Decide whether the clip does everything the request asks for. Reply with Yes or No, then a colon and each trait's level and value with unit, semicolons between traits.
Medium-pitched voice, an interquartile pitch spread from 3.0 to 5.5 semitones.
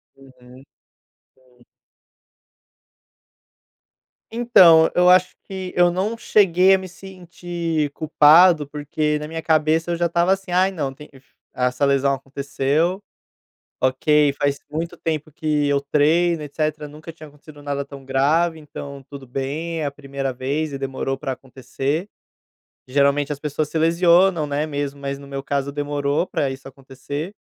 Yes: medium, 150 Hz; average, 3.3 semitones